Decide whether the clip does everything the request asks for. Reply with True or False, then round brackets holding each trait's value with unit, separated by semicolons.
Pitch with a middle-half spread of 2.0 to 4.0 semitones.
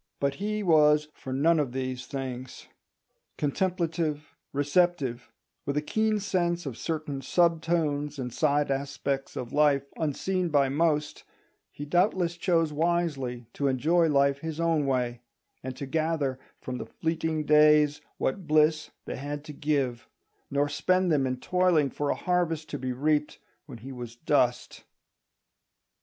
True (3.3 semitones)